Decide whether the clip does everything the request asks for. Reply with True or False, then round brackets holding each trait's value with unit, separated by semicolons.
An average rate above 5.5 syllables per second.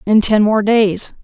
False (3.8 syllables/s)